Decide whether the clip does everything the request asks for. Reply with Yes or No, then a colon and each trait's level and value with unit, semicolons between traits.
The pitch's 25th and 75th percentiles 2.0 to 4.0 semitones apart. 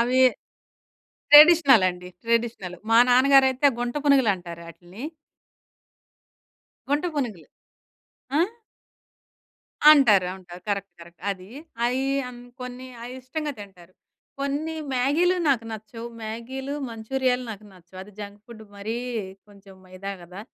No: wide, 5.4 semitones